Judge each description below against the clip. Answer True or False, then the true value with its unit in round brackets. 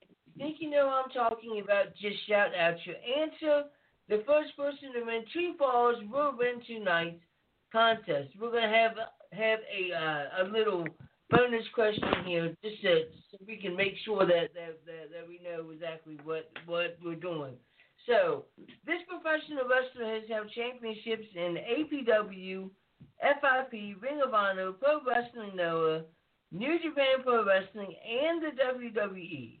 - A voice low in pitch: False (220 Hz)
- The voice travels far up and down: True (6.7 semitones)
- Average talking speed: True (150 wpm)